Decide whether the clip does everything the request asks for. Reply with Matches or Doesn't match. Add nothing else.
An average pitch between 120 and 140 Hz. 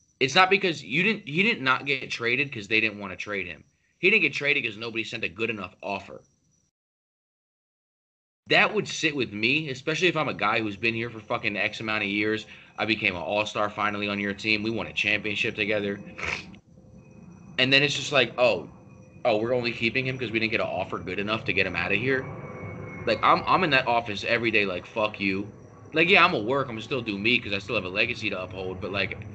Doesn't match